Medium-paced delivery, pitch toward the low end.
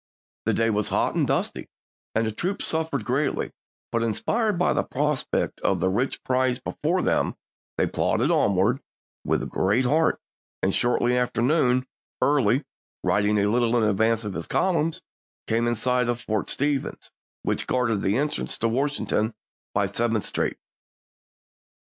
Yes: average, 155 wpm; low, 120 Hz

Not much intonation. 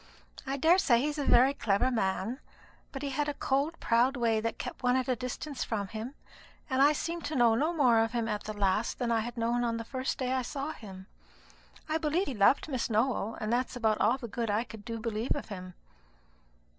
No: average, 3.5 semitones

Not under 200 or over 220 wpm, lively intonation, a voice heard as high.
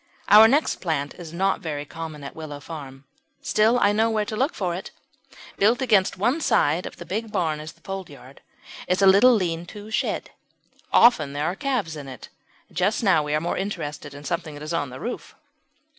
No: fast, 205 wpm; wide, 5.8 semitones; medium, 175 Hz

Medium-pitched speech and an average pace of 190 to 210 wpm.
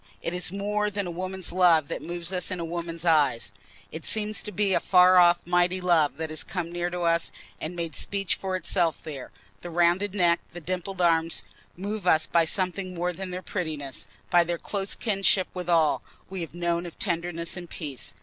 Yes: medium, 175 Hz; average, 200 wpm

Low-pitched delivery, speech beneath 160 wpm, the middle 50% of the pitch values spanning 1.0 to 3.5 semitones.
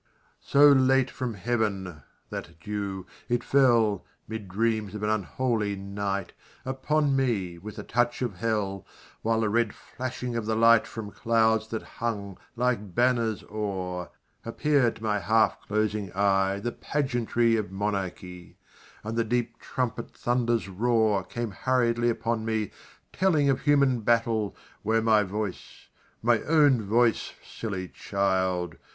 Yes: low, 110 Hz; average, 140 wpm; average, 3.1 semitones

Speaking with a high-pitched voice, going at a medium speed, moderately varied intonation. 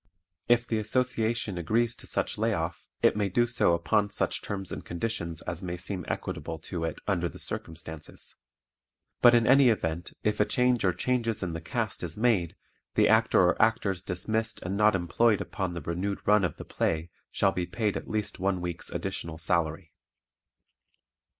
No: very low, 95 Hz; average, 180 wpm; average, 4.5 semitones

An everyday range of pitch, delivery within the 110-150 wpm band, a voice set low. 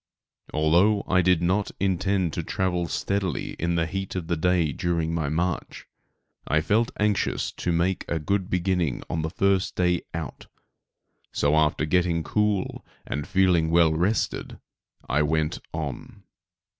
Yes: average, 3.0 semitones; average, 145 wpm; very low, 85 Hz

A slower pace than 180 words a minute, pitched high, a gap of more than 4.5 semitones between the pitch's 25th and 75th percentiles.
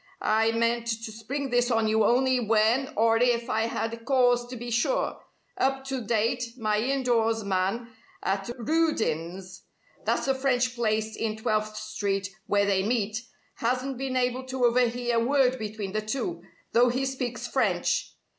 No: average, 160 wpm; high, 235 Hz; narrow, 2.6 semitones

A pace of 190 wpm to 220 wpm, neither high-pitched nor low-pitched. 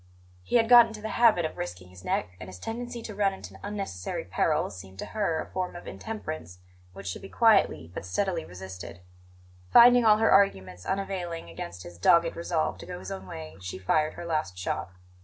Yes: average, 200 wpm; medium, 155 Hz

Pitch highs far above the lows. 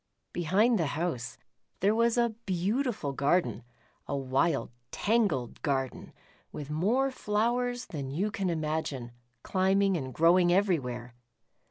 Yes: wide, 7.0 semitones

